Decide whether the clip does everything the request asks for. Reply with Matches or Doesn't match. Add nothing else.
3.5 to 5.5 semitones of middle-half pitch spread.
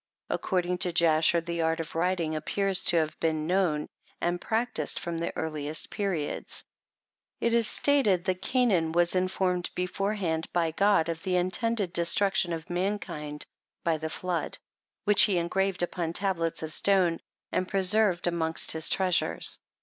Doesn't match